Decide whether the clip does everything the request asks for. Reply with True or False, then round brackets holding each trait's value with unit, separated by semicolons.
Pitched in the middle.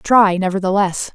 False (195 Hz)